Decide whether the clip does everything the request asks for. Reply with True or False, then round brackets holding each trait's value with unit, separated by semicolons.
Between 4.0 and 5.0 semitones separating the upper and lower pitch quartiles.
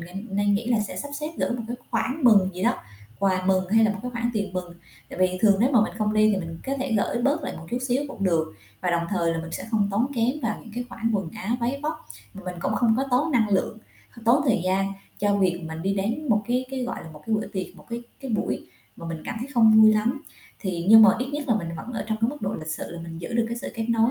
True (4.5 semitones)